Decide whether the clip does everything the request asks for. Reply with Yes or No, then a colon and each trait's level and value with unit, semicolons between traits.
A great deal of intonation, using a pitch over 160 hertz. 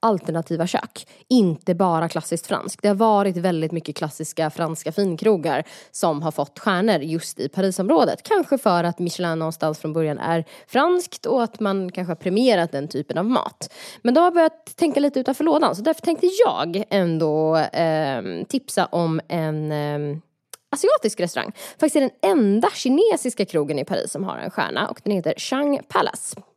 Yes: wide, 7.4 semitones; medium, 185 Hz